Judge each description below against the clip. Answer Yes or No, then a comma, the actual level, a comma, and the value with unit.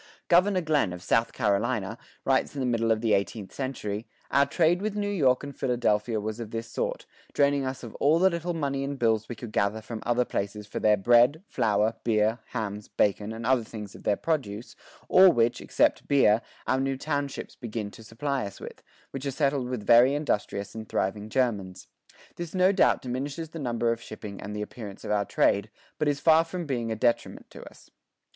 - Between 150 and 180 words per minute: No, fast, 205 wpm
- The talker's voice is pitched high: No, low, 120 Hz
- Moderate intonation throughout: Yes, average, 4.8 semitones